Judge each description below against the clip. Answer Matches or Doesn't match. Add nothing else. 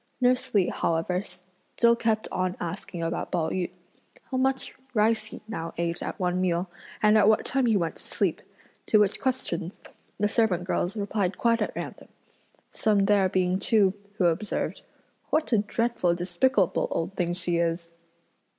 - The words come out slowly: Doesn't match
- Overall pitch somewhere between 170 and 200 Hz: Matches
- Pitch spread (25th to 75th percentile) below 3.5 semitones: Doesn't match